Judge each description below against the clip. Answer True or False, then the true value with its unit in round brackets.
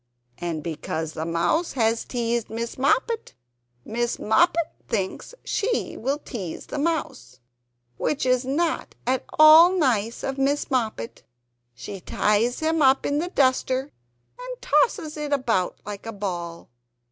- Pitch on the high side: True (255 Hz)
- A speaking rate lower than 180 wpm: True (135 wpm)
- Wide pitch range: True (6.9 semitones)